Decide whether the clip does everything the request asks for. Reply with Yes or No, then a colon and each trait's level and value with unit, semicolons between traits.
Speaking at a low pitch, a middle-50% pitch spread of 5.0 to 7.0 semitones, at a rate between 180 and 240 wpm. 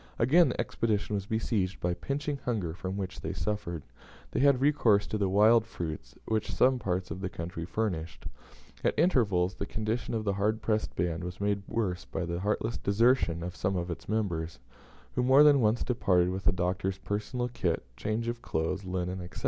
No: low, 100 Hz; average, 4.3 semitones; average, 190 wpm